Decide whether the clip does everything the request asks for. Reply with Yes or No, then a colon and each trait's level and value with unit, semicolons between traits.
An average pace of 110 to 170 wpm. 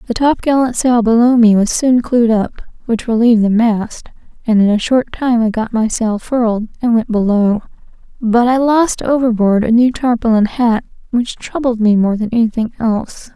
No: average, 190 wpm